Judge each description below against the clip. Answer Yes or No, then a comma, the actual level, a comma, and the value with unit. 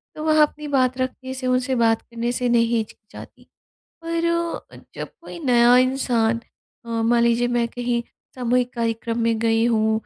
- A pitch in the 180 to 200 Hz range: No, high, 240 Hz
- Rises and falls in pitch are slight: Yes, narrow, 1.9 semitones